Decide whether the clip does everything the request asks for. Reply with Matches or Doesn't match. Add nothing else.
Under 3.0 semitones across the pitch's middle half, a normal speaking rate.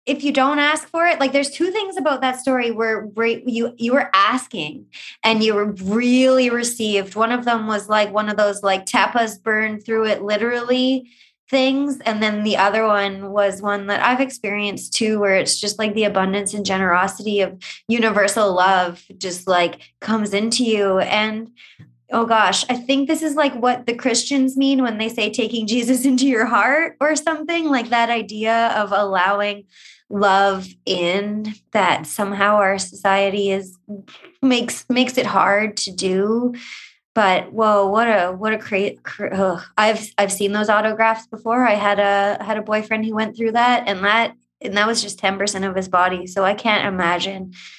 Doesn't match